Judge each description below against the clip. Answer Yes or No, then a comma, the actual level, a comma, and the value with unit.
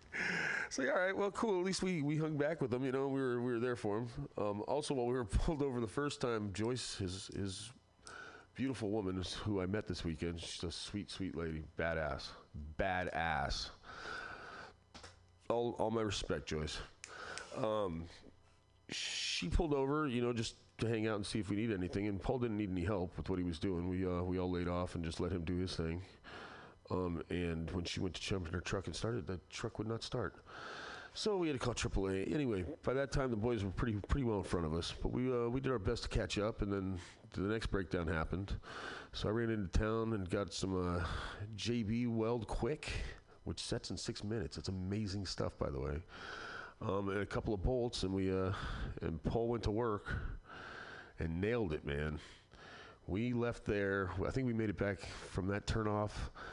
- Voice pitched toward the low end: Yes, low, 100 Hz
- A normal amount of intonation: Yes, average, 4.5 semitones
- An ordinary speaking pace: No, fast, 215 wpm